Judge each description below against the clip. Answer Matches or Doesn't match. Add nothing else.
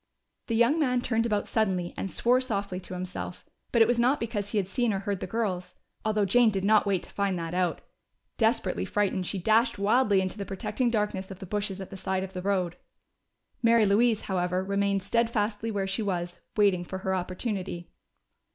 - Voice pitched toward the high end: Matches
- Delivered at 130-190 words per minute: Doesn't match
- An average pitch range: Matches